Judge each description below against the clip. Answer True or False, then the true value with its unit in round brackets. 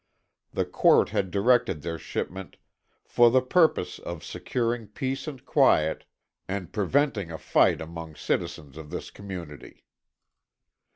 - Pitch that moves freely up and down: True (6.8 semitones)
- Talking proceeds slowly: True (125 wpm)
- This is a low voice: True (95 Hz)